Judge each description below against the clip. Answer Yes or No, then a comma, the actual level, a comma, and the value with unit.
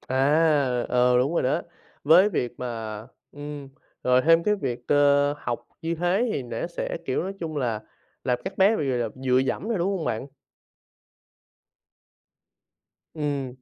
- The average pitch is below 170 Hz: Yes, medium, 140 Hz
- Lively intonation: No, average, 4.7 semitones